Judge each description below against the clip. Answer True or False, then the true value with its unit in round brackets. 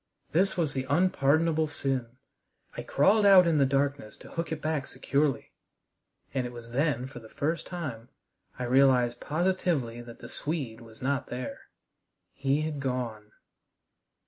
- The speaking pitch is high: False (140 Hz)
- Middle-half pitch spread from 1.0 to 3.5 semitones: False (4.3 semitones)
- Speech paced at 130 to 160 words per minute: True (150 wpm)